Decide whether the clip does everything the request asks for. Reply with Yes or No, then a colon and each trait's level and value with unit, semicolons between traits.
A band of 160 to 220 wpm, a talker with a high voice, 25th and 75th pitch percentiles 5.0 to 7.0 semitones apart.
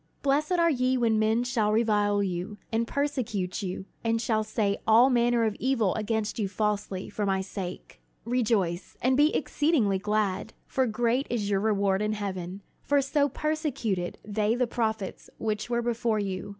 No: average, 165 wpm; high, 220 Hz; average, 3.3 semitones